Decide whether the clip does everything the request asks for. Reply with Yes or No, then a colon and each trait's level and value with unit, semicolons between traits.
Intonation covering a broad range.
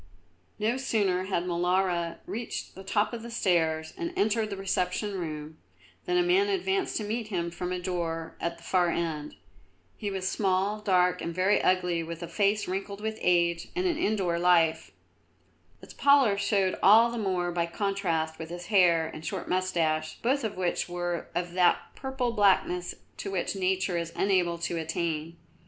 No: average, 3.4 semitones